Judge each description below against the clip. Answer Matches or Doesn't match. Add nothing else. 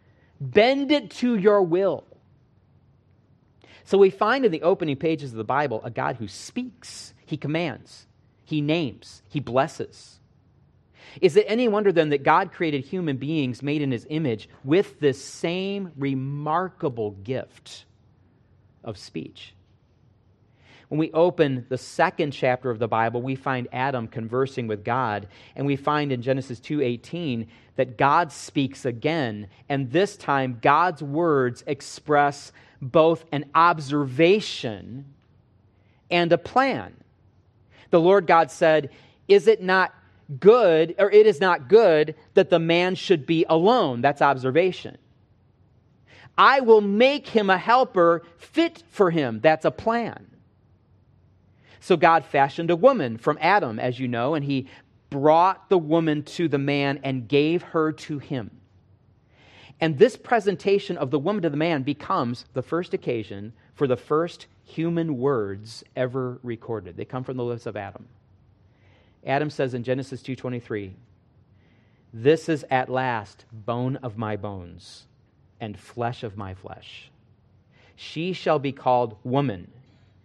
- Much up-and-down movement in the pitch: Matches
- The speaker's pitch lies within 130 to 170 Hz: Matches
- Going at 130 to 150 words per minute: Matches